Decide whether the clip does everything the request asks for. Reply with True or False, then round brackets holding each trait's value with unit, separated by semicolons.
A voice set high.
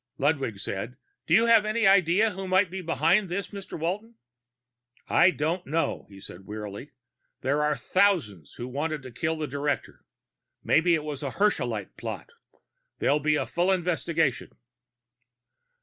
False (165 Hz)